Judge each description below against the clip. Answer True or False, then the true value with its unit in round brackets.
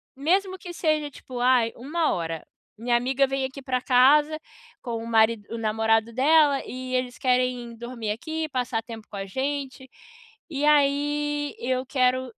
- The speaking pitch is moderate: False (255 Hz)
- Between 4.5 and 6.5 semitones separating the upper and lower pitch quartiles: False (3.6 semitones)